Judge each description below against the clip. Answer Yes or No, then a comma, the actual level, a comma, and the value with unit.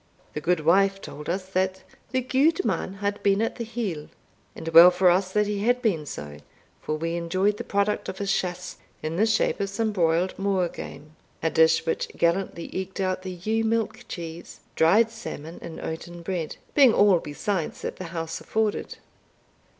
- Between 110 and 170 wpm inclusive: No, average, 180 wpm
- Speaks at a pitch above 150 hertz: Yes, medium, 185 Hz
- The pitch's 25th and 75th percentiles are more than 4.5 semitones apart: No, average, 3.7 semitones